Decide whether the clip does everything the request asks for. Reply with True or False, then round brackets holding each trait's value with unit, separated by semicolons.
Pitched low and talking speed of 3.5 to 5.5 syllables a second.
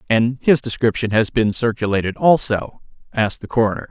False (115 Hz; 5.8 syllables/s)